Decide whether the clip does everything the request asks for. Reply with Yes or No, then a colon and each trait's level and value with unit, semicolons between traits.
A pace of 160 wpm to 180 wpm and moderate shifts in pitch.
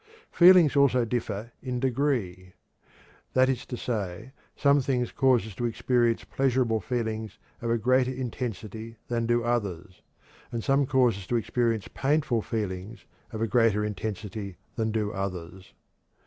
No: average, 145 wpm; average, 3.2 semitones